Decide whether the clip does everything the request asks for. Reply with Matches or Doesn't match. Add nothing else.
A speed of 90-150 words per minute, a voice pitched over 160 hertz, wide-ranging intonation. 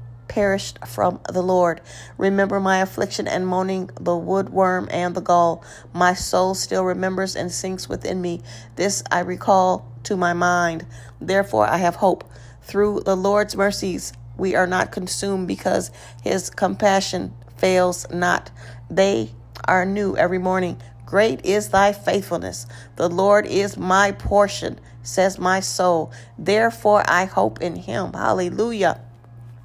Matches